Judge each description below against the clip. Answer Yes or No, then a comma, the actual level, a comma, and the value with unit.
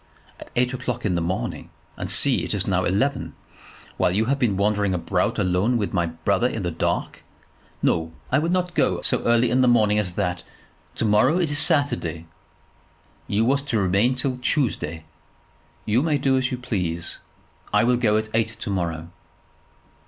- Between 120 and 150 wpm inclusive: No, average, 175 wpm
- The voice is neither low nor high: No, low, 110 Hz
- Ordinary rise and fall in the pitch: No, wide, 5.7 semitones